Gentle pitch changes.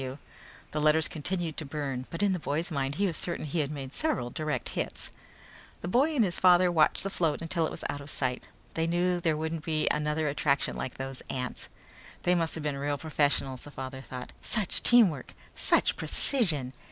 No: average, 3.8 semitones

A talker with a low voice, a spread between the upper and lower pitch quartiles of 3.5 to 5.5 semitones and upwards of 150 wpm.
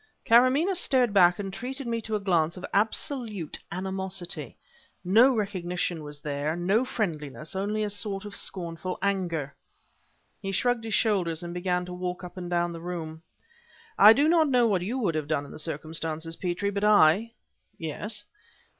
No: high, 190 Hz; average, 4.2 semitones; average, 175 wpm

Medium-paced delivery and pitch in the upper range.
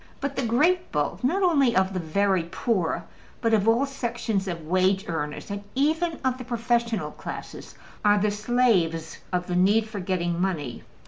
Yes: average, 175 wpm; high, 205 Hz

